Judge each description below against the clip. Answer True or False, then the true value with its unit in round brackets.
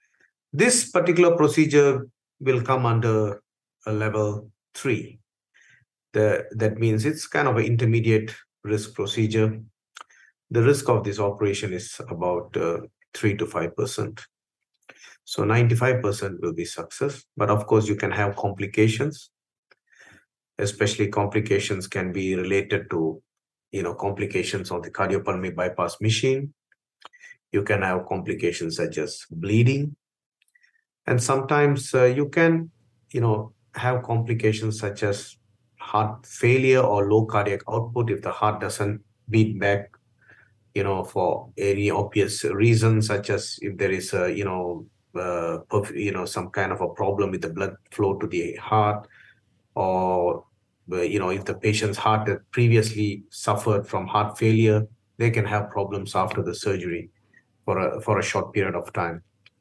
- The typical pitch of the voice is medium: False (110 Hz)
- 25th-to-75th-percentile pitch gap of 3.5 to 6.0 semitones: False (3.0 semitones)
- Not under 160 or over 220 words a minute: False (145 wpm)